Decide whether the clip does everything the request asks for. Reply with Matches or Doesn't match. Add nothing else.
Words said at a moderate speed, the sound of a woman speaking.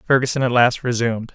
Doesn't match